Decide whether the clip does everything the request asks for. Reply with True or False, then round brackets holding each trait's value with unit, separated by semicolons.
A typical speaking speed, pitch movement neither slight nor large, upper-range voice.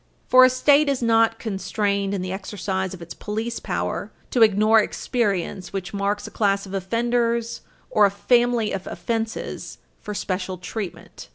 True (160 wpm; 3.2 semitones; 210 Hz)